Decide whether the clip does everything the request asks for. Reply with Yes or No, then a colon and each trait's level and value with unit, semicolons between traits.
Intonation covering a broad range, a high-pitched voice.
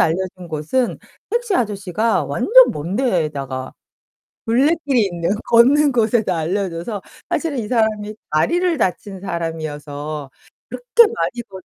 Yes: wide, 7.2 semitones; high, 205 Hz